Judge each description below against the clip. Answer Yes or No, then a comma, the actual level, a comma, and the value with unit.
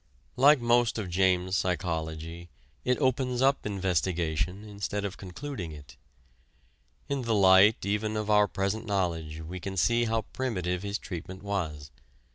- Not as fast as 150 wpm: Yes, average, 140 wpm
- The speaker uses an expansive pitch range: No, average, 3.9 semitones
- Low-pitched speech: Yes, very low, 95 Hz